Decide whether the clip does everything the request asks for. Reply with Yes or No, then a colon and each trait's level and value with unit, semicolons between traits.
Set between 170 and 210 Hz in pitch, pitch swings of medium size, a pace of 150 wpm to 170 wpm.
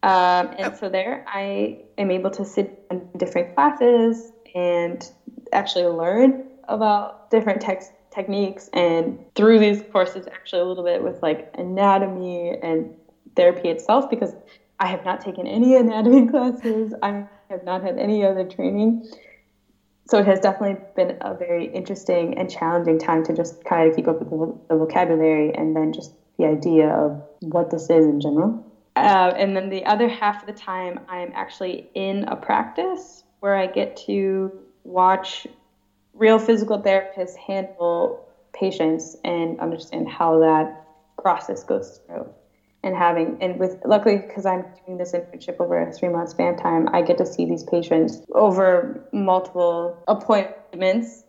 Yes: medium, 185 Hz; average, 3.5 semitones; average, 160 wpm